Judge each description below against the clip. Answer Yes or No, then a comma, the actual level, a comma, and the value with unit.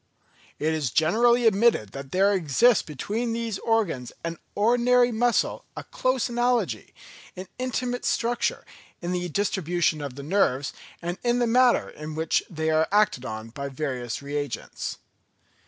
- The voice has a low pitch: No, medium, 185 Hz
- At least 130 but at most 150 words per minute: Yes, average, 145 wpm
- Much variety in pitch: Yes, wide, 7.9 semitones